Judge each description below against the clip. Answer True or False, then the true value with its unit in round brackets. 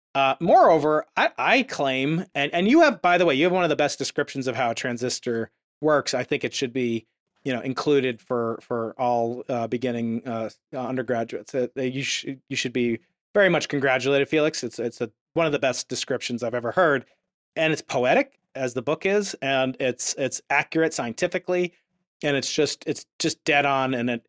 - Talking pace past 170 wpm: True (205 wpm)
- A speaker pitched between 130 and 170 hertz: True (135 Hz)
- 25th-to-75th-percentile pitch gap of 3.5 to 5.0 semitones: True (4.1 semitones)